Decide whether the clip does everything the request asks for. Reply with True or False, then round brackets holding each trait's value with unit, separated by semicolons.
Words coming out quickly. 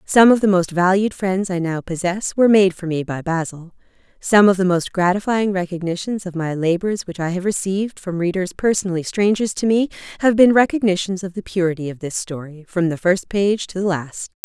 True (210 wpm)